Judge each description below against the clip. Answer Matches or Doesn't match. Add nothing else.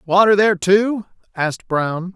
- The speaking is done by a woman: Doesn't match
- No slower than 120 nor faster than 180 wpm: Matches